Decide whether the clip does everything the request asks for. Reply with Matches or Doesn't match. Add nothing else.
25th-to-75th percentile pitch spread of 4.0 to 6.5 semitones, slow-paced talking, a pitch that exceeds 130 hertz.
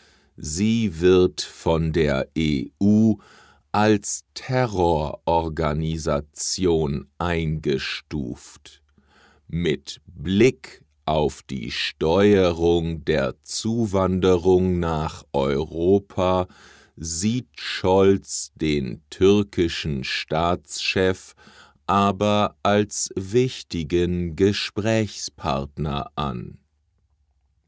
Doesn't match